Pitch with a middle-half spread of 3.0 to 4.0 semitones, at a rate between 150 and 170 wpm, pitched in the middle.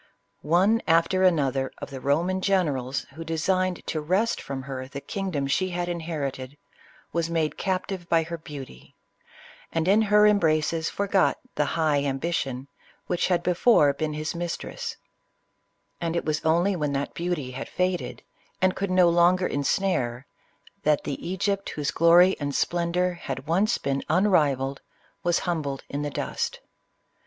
No: average, 4.4 semitones; average, 155 wpm; medium, 165 Hz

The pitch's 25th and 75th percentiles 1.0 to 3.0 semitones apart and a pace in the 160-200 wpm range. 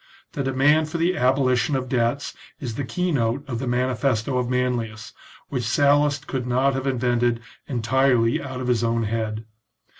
Yes: average, 2.7 semitones; average, 170 wpm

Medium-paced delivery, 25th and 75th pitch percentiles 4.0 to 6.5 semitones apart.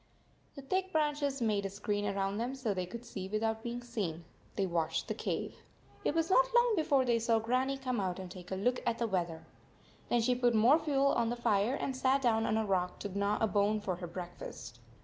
No: fast, 230 wpm; average, 5.0 semitones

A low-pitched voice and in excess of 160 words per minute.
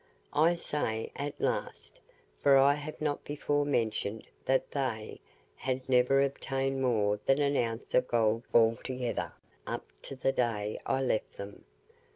No: low, 130 Hz; average, 145 wpm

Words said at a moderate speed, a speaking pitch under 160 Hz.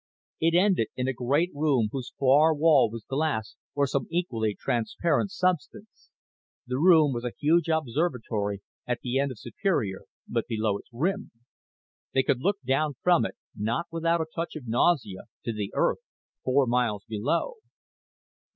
Yes: average, 160 wpm; low, 135 Hz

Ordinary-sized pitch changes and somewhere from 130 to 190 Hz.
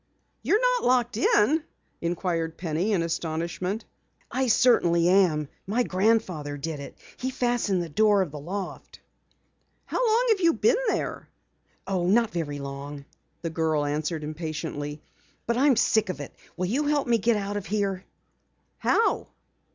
No: wide, 6.6 semitones; medium, 185 Hz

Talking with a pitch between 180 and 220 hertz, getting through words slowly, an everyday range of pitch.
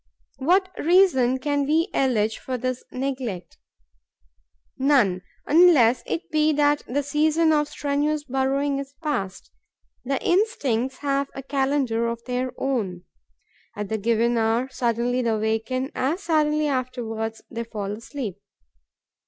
No: very high, 265 Hz; slow, 130 wpm; average, 4.0 semitones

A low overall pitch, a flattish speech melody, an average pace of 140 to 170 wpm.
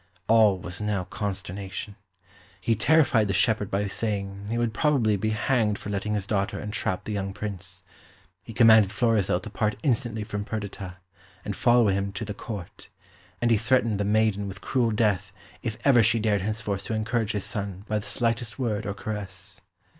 No: low, 105 Hz; narrow, 2.3 semitones; average, 180 wpm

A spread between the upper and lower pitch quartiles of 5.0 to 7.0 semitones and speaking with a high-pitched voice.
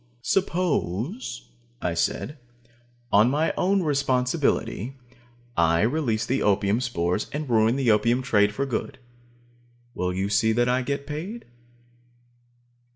No: wide, 5.4 semitones; low, 125 Hz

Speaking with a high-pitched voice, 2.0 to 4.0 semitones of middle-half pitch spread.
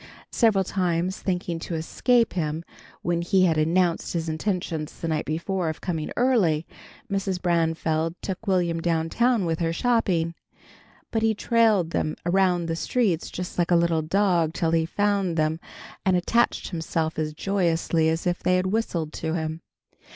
No: medium, 170 Hz; average, 2.9 semitones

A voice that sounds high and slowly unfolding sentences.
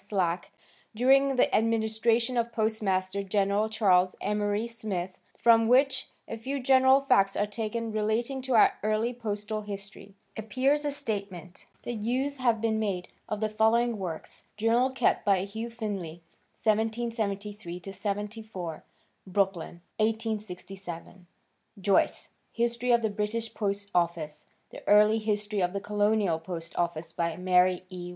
Yes: high, 210 Hz; slow, 130 wpm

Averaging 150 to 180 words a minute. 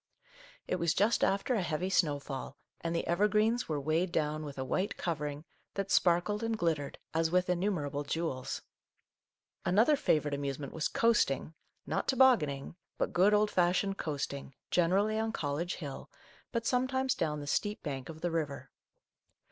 Yes: average, 165 wpm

